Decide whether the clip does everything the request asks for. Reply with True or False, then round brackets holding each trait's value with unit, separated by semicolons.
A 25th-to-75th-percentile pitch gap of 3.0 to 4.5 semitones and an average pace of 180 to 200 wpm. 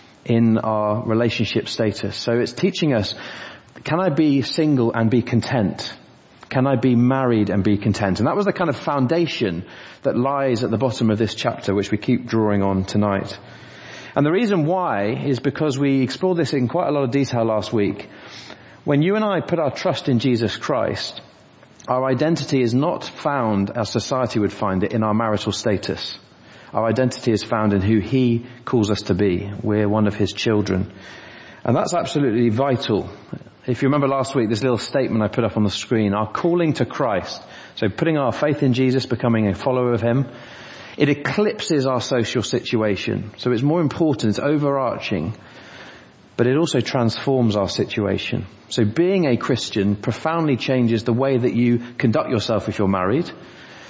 True (4.1 semitones; 185 wpm)